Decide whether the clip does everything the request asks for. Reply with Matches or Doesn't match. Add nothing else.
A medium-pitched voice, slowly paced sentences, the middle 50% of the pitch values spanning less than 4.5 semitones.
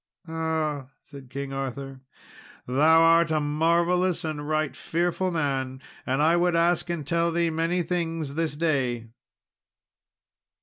Matches